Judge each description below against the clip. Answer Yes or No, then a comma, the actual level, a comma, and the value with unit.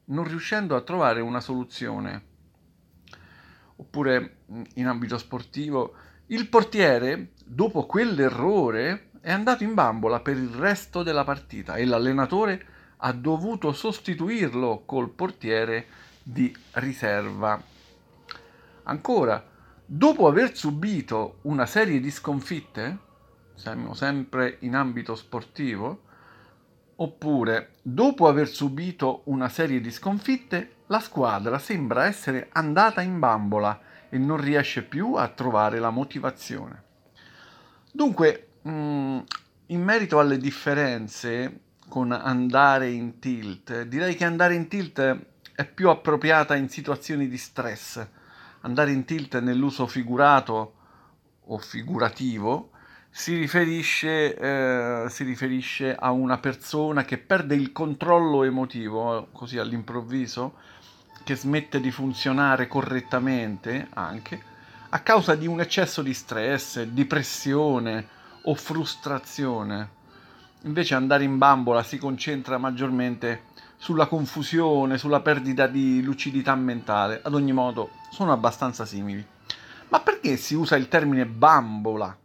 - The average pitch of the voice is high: No, low, 135 Hz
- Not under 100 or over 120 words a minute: Yes, slow, 115 wpm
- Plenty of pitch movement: No, average, 4.1 semitones